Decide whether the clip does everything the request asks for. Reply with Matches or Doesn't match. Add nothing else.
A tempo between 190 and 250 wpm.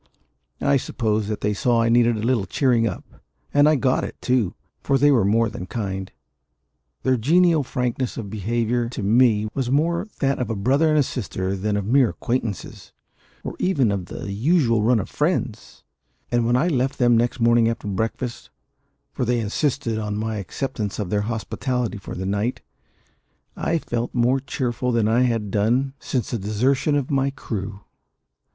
Doesn't match